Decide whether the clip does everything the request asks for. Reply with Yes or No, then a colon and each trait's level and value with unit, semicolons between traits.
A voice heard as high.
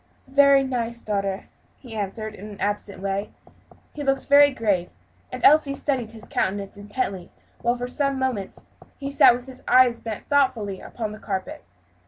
Yes: high, 230 Hz